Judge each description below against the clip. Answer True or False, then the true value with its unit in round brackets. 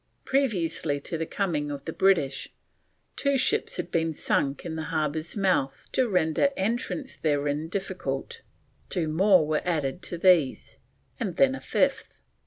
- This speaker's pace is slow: False (150 wpm)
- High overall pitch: False (165 Hz)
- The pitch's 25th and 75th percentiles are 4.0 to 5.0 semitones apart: True (4.6 semitones)